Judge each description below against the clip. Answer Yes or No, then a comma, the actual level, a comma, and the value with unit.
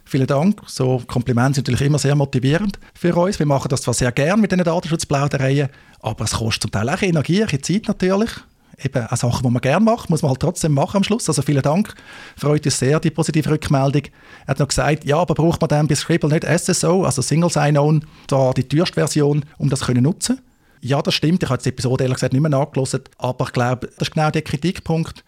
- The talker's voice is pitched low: No, medium, 145 Hz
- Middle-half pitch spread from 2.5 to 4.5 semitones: Yes, average, 3.9 semitones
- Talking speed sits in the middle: No, fast, 225 wpm